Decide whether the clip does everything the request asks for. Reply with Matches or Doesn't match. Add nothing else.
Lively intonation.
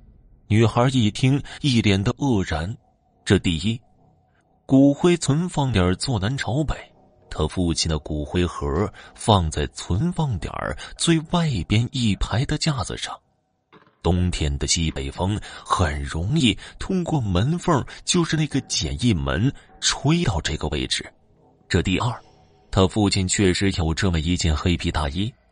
Matches